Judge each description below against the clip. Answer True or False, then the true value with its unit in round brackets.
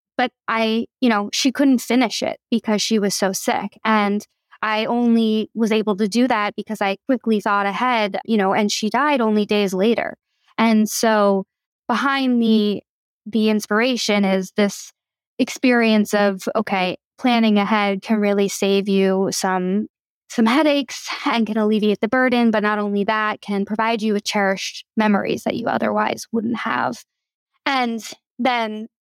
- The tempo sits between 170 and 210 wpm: False (155 wpm)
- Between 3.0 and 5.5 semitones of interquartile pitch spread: False (2.6 semitones)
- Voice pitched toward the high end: True (220 Hz)